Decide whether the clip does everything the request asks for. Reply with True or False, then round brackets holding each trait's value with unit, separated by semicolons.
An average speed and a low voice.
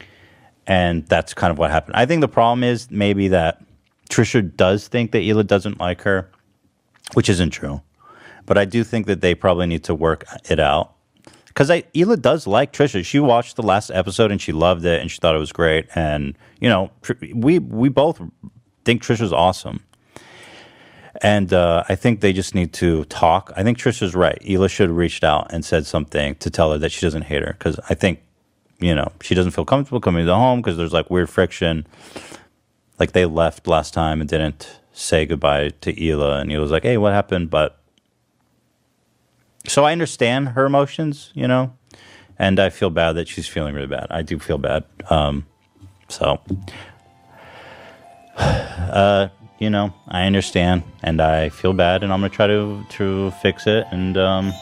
True (190 wpm; 95 Hz)